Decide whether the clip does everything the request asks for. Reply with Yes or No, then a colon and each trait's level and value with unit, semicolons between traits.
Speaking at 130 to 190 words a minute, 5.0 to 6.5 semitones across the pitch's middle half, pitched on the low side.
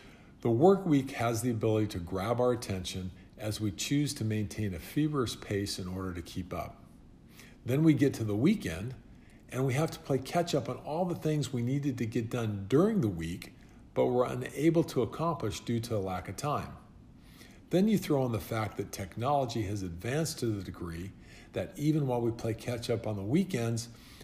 No: fast, 205 wpm; wide, 5.5 semitones; low, 115 Hz